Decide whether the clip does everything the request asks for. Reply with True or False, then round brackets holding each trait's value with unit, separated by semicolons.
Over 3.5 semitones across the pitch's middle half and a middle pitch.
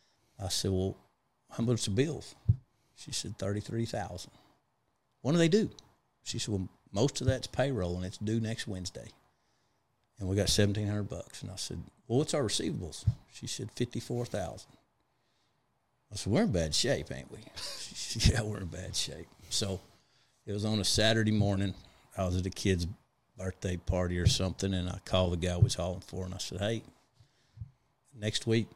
False (4.3 semitones; 105 Hz)